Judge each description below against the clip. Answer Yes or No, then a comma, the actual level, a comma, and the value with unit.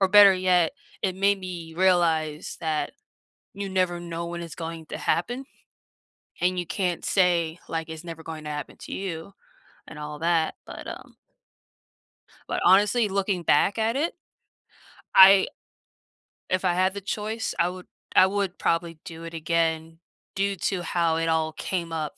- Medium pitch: Yes, medium, 175 Hz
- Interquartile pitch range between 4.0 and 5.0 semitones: No, average, 2.8 semitones